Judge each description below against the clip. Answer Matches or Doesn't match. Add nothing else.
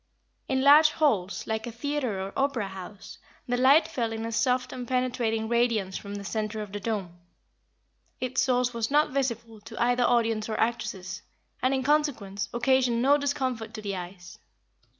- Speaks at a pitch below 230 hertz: Doesn't match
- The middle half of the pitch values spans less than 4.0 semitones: Matches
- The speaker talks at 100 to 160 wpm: Doesn't match